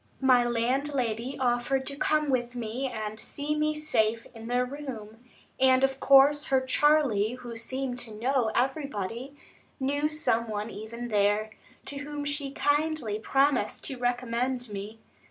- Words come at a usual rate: Yes, average, 145 wpm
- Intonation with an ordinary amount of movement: Yes, average, 3.5 semitones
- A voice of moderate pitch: No, very high, 250 Hz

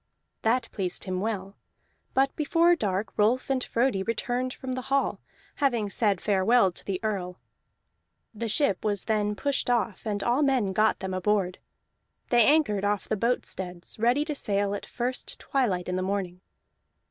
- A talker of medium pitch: No, high, 215 Hz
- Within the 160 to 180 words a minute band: Yes, average, 165 wpm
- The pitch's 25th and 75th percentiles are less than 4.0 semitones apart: No, average, 4.6 semitones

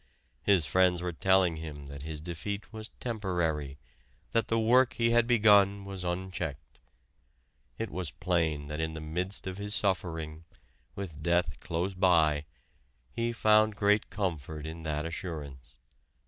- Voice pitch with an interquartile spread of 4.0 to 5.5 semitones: Yes, average, 4.5 semitones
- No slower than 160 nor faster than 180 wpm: No, average, 145 wpm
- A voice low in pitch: Yes, very low, 90 Hz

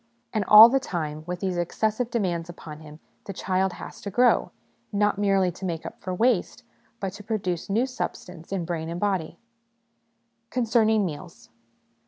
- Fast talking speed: No, average, 165 wpm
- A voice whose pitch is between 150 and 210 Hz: Yes, high, 190 Hz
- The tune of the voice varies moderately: Yes, average, 3.8 semitones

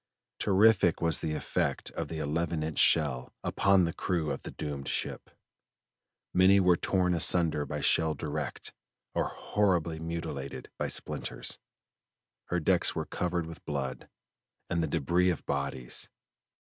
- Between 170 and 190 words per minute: No, average, 140 wpm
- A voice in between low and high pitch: No, very low, 80 Hz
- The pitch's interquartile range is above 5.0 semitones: No, average, 3.2 semitones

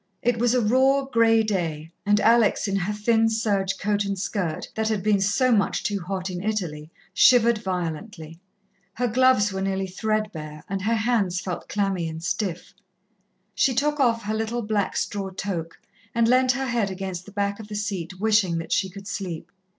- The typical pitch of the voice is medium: No, high, 205 Hz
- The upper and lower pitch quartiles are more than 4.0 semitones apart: No, average, 3.2 semitones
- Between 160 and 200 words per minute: Yes, average, 190 wpm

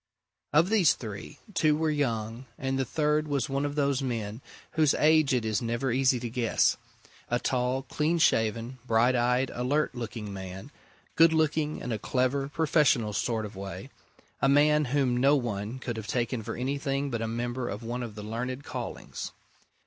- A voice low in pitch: Yes, low, 125 Hz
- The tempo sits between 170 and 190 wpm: Yes, average, 180 wpm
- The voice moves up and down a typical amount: Yes, average, 3.8 semitones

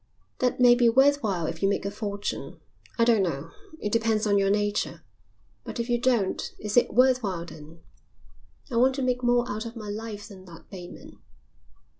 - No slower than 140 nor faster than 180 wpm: No, average, 195 wpm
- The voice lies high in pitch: Yes, high, 215 Hz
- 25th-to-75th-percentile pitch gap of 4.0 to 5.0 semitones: No, average, 3.6 semitones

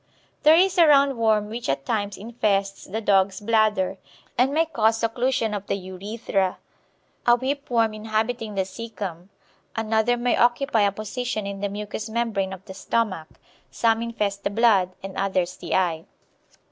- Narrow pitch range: No, average, 3.1 semitones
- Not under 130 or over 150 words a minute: No, average, 160 wpm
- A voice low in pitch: No, high, 215 Hz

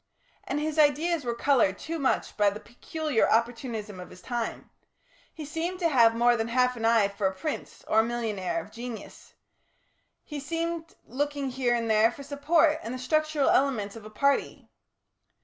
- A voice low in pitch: No, very high, 250 Hz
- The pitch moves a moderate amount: Yes, average, 4.9 semitones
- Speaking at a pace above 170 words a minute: Yes, average, 180 wpm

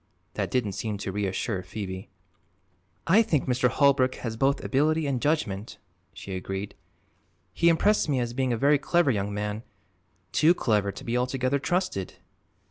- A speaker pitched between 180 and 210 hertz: No, low, 125 Hz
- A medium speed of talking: Yes, average, 155 wpm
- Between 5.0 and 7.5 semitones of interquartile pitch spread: Yes, wide, 5.6 semitones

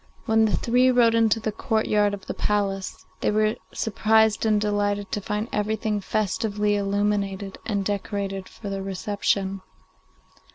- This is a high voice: Yes, high, 210 Hz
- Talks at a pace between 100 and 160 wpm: Yes, average, 140 wpm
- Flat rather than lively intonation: Yes, narrow, 1.5 semitones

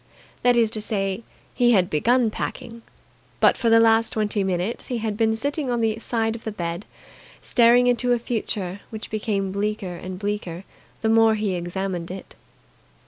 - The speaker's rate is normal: Yes, average, 175 wpm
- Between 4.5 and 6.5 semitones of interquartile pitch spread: No, average, 3.1 semitones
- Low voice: No, high, 220 Hz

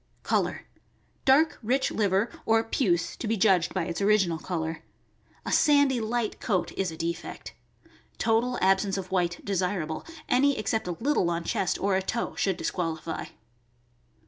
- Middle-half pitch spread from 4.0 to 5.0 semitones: Yes, average, 4.5 semitones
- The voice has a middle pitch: No, high, 195 Hz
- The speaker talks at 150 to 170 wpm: Yes, average, 160 wpm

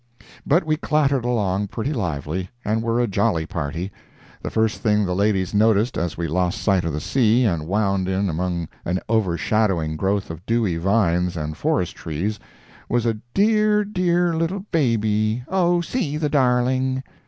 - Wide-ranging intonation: Yes, wide, 6.3 semitones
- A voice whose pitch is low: Yes, low, 110 Hz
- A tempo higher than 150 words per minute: Yes, average, 160 wpm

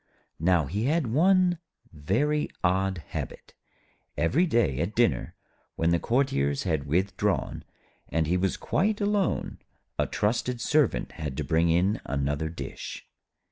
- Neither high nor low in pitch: No, very low, 95 Hz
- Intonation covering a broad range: Yes, wide, 8.8 semitones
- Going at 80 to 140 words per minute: Yes, slow, 135 wpm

